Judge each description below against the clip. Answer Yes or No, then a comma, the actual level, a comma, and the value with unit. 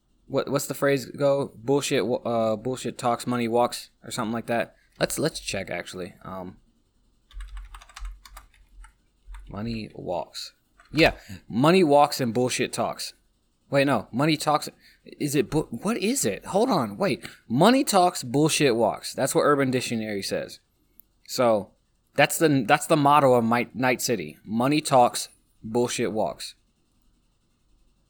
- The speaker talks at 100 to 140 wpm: Yes, slow, 135 wpm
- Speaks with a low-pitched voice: Yes, low, 125 Hz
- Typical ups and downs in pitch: Yes, average, 3.7 semitones